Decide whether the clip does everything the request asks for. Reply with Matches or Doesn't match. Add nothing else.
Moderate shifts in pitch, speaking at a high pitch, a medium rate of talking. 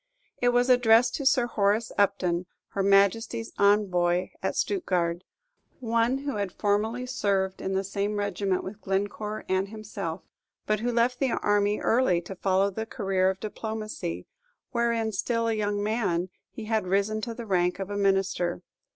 Matches